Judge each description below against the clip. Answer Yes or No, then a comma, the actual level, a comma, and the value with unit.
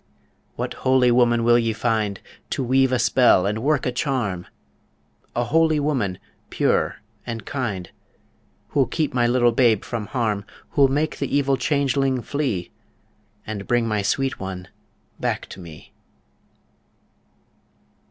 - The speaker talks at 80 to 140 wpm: Yes, slow, 135 wpm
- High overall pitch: No, low, 120 Hz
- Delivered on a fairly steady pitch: No, average, 3.9 semitones